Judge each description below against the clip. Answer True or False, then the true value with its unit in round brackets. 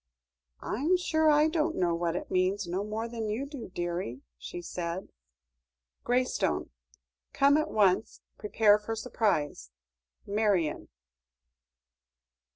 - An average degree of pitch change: False (6.4 semitones)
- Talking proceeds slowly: True (115 wpm)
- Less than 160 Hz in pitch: False (210 Hz)